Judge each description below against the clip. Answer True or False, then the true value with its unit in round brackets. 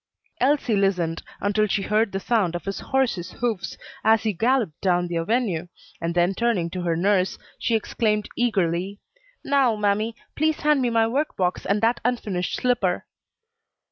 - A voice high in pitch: True (205 Hz)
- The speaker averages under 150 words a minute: False (165 wpm)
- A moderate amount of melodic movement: True (4.6 semitones)